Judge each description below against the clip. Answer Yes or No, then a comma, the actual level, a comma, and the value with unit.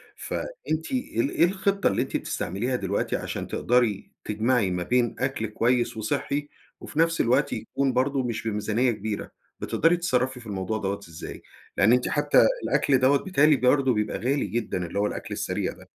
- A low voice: Yes, low, 125 Hz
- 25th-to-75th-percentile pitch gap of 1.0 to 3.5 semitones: No, average, 4.8 semitones